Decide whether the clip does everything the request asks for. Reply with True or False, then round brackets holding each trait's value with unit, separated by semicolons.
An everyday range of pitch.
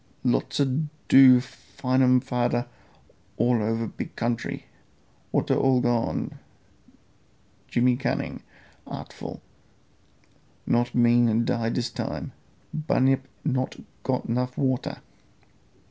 False (1.4 semitones)